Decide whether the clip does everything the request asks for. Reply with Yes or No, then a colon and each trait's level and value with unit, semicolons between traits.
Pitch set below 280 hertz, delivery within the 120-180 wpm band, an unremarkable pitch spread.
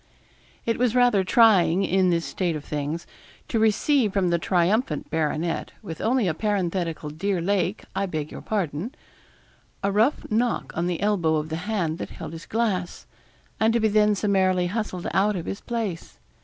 Yes: high, 190 Hz; average, 175 wpm; average, 4.3 semitones